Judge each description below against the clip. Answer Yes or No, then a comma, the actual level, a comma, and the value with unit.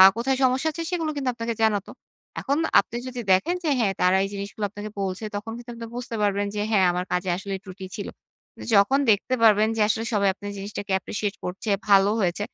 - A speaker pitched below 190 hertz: No, high, 205 Hz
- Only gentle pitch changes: No, average, 3.2 semitones